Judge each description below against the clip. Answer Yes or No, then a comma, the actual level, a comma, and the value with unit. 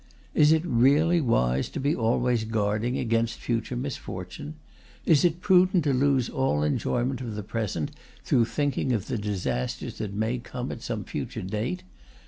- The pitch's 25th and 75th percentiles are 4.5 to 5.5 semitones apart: Yes, average, 5.0 semitones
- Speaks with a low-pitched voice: Yes, low, 120 Hz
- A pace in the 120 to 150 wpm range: No, average, 160 wpm